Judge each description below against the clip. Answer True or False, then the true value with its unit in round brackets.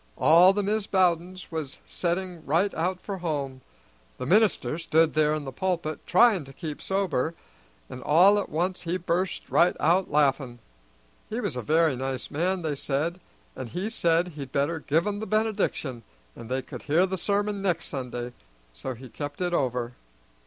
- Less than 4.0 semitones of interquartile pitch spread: False (4.8 semitones)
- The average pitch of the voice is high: False (165 Hz)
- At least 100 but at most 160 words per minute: False (175 wpm)